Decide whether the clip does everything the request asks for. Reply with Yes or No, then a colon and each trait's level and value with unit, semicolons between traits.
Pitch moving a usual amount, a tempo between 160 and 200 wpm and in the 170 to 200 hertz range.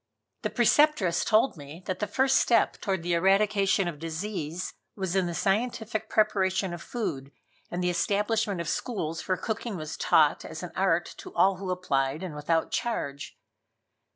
Yes: average, 4.2 semitones; average, 165 wpm; high, 190 Hz